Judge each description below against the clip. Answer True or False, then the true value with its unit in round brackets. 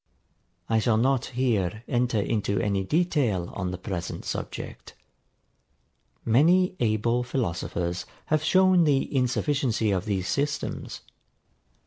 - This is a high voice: False (115 Hz)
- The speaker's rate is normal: False (110 wpm)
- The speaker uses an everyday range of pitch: False (5.9 semitones)